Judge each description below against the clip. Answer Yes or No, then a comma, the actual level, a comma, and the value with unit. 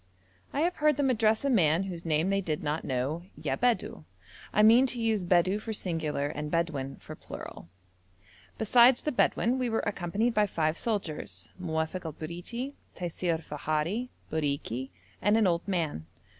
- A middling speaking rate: Yes, average, 170 wpm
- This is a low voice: No, medium, 175 Hz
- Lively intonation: Yes, wide, 6.2 semitones